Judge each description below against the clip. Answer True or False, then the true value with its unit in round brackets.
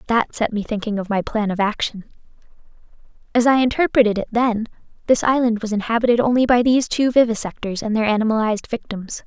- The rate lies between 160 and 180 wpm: True (175 wpm)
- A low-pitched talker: False (225 Hz)